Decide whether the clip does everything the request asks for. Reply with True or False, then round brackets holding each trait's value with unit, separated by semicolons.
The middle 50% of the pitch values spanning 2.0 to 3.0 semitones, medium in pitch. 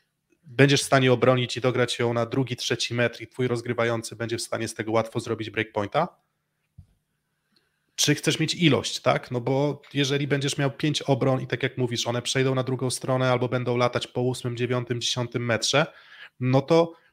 False (2.7 semitones; 125 Hz)